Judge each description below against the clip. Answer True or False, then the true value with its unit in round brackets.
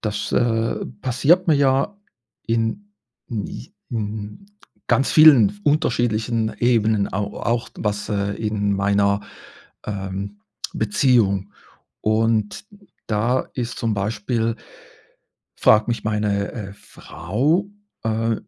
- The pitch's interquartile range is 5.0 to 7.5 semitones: False (2.8 semitones)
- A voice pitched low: True (110 Hz)